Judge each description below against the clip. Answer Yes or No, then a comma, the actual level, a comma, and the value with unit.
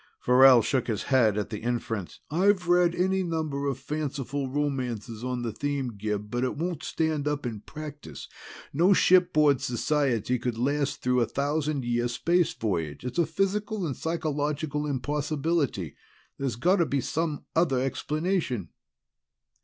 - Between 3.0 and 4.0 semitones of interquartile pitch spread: No, average, 4.5 semitones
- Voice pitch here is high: No, medium, 140 Hz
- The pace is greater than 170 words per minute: No, average, 150 wpm